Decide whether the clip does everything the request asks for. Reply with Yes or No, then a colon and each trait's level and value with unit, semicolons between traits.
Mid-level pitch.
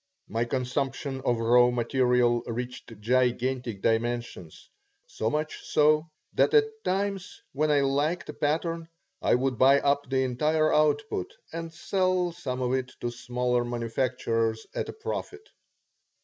No: low, 130 Hz